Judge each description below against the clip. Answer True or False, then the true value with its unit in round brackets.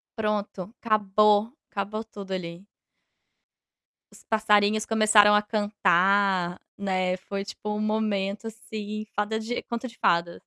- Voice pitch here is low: False (210 Hz)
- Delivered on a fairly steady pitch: True (1.6 semitones)